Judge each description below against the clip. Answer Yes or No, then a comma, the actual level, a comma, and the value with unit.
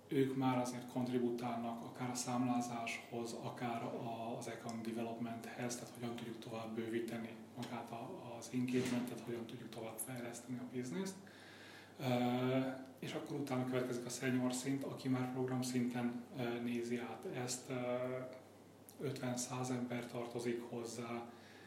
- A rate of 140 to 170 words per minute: No, average, 120 wpm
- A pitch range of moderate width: No, narrow, 1.3 semitones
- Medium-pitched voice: No, low, 120 Hz